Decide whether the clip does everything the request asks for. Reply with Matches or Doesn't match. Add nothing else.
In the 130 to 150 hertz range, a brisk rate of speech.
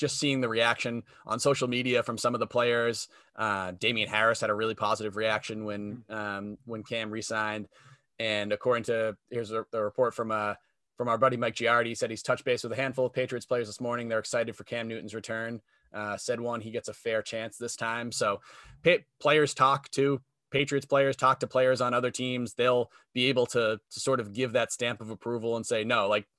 Doesn't match